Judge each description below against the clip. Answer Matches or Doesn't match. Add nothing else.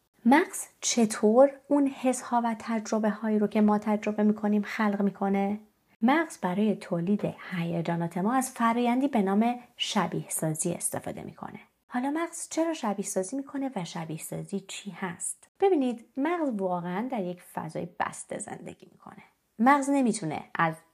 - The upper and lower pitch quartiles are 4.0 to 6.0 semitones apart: Matches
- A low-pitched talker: Doesn't match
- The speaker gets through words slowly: Doesn't match